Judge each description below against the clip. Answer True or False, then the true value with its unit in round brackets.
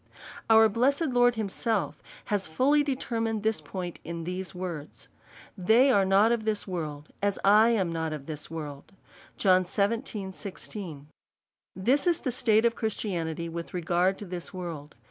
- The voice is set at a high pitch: True (195 Hz)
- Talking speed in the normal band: True (145 wpm)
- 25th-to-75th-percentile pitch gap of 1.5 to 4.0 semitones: False (4.9 semitones)